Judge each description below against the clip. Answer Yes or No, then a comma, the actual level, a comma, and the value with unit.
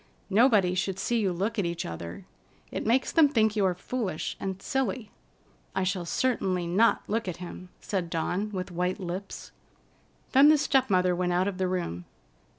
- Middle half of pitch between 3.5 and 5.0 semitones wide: Yes, average, 3.9 semitones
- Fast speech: No, average, 180 wpm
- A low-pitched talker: No, high, 190 Hz